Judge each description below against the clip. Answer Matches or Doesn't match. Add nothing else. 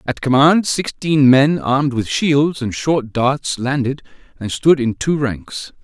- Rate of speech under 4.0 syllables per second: Matches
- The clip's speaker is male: Matches